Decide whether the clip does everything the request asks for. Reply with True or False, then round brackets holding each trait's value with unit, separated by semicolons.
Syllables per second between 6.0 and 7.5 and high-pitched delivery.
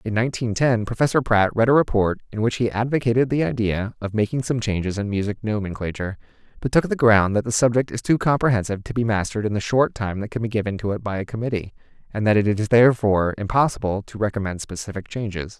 False (6.5 syllables/s; 110 Hz)